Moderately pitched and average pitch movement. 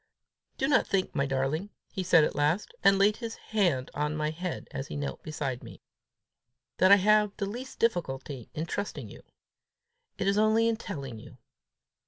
No: medium, 180 Hz; wide, 6.3 semitones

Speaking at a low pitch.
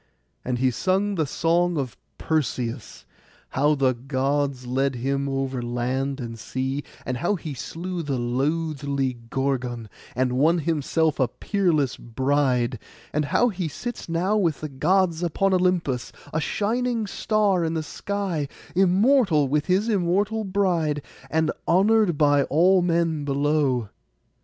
No: medium, 150 Hz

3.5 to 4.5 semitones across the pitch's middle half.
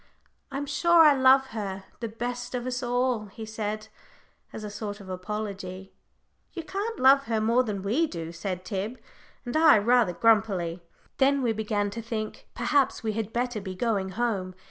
Yes: average, 3.8 semitones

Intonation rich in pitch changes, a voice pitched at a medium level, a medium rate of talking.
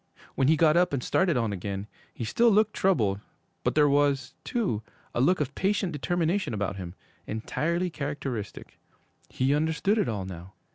Yes: wide, 8.1 semitones; medium, 145 Hz; average, 170 wpm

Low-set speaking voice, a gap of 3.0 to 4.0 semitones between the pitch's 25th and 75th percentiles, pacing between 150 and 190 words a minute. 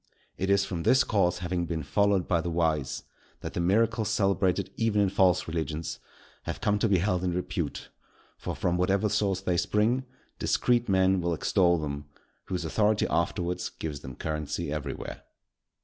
Yes: very low, 90 Hz; average, 3.4 semitones; average, 165 wpm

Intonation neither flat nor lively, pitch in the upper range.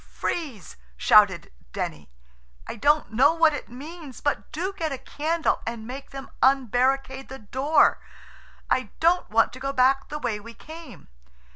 Yes: average, 4.4 semitones; very high, 270 Hz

